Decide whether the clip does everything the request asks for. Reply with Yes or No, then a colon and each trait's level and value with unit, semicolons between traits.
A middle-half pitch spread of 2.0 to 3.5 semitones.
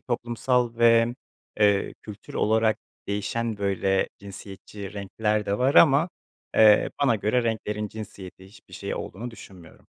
Yes: average, 2.7 semitones